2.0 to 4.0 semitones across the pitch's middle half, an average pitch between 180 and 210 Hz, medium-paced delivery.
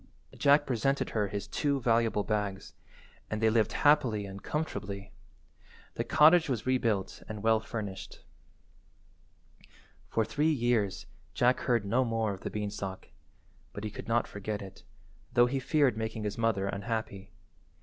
No: average, 3.3 semitones; low, 110 Hz; average, 145 wpm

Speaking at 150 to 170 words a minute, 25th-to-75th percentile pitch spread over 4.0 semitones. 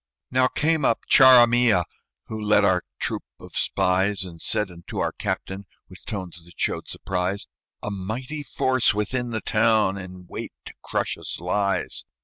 Yes: average, 155 wpm; average, 4.5 semitones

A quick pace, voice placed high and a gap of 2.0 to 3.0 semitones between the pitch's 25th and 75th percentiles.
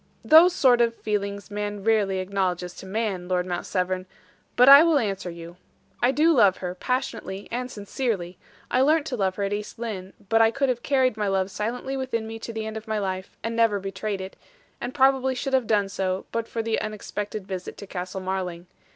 No: fast, 210 wpm; high, 210 Hz; average, 4.3 semitones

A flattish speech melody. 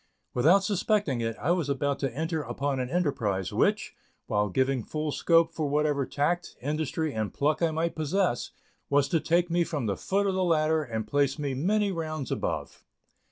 No: average, 3.8 semitones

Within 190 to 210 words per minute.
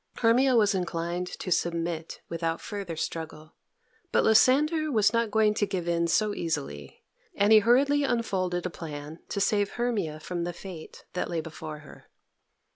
No: average, 160 wpm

